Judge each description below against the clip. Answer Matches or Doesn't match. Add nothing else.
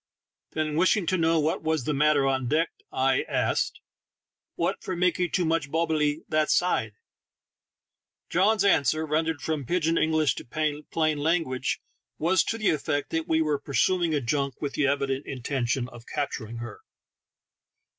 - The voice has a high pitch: Doesn't match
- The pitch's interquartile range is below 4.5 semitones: Matches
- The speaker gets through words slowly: Doesn't match